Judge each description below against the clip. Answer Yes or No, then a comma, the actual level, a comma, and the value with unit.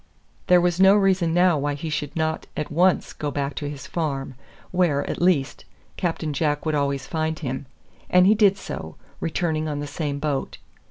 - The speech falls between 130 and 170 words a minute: No, average, 185 wpm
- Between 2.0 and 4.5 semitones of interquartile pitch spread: Yes, average, 3.6 semitones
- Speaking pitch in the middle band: Yes, medium, 155 Hz